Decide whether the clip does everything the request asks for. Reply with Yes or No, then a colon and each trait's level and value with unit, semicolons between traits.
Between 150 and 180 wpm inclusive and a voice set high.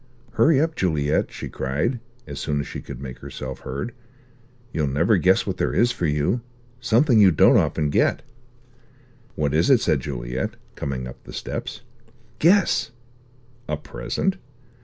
No: average, 155 wpm; very low, 75 Hz